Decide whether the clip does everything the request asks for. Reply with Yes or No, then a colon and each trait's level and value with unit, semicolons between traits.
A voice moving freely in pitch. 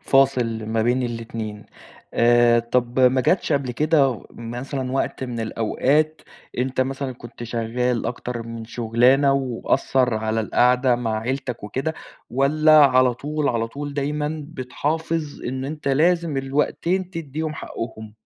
No: average, 3.3 semitones